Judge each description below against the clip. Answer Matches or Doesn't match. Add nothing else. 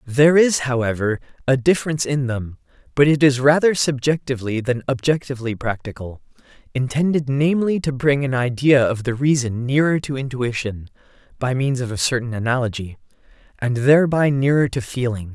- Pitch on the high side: Doesn't match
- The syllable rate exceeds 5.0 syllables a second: Matches